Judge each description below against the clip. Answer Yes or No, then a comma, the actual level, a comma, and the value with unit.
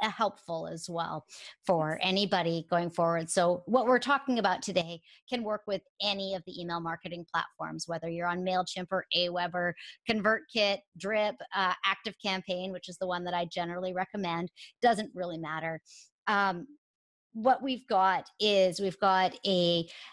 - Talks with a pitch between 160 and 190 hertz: Yes, medium, 185 Hz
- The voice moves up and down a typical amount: Yes, average, 3.1 semitones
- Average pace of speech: Yes, average, 155 wpm